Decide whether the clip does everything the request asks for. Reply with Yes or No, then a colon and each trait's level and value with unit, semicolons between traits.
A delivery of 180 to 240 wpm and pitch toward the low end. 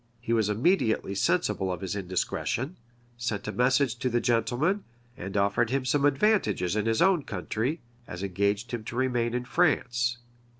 No: average, 165 wpm; low, 120 Hz